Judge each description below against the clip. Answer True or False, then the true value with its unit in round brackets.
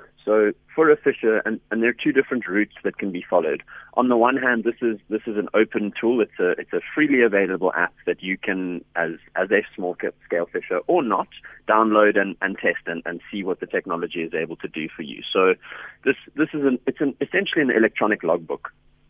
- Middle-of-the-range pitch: False (110 Hz)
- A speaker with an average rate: False (225 wpm)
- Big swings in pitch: True (7.2 semitones)